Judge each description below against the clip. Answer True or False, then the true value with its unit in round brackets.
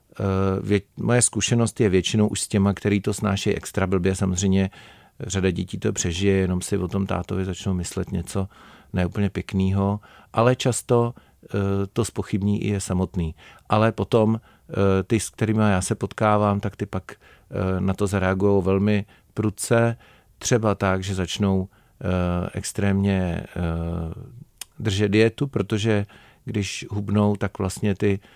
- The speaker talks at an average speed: True (150 wpm)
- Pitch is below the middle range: True (100 Hz)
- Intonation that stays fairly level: True (2.1 semitones)